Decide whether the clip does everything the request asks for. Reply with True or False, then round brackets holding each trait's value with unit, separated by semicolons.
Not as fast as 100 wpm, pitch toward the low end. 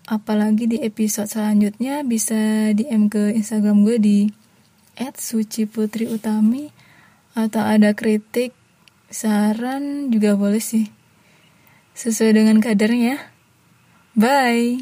False (90 wpm; 220 Hz)